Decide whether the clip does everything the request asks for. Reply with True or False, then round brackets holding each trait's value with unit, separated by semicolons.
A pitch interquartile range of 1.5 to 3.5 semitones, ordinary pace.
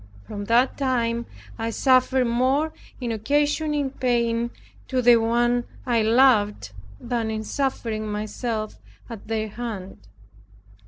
False (2.8 semitones; 110 wpm)